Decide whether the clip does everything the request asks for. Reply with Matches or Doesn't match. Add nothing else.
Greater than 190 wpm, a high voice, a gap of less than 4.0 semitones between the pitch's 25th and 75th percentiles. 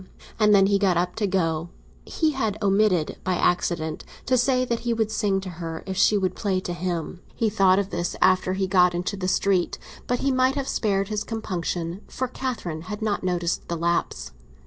Matches